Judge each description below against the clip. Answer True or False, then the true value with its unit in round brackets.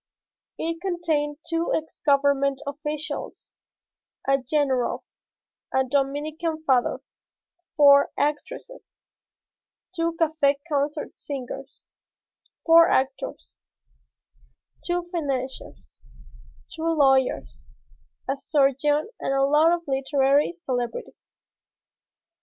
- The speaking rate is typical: False (85 wpm)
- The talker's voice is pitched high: True (290 Hz)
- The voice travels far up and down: False (2.8 semitones)